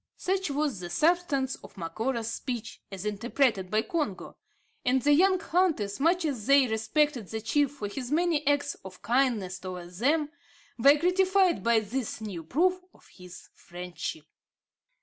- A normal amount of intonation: No, wide, 6.8 semitones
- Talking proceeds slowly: No, average, 150 wpm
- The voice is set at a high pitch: Yes, very high, 260 Hz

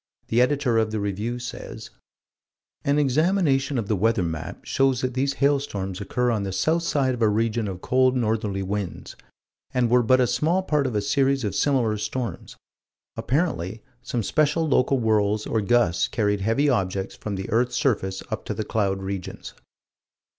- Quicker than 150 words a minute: Yes, average, 175 wpm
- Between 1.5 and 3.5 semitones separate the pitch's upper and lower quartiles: No, average, 4.7 semitones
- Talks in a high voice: No, low, 115 Hz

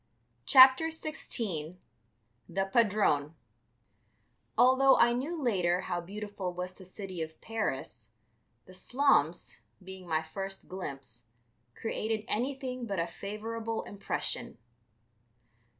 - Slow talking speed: Yes, slow, 105 wpm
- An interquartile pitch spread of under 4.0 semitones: No, average, 5.2 semitones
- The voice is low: No, high, 195 Hz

